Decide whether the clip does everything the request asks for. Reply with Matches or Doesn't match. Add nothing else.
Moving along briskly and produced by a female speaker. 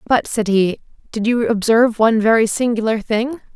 Doesn't match